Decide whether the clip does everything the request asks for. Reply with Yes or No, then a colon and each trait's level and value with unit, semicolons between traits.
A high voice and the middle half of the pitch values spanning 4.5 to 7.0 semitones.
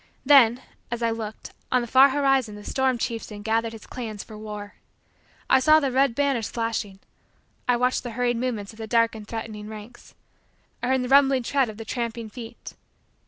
No: high, 235 Hz; average, 2.8 semitones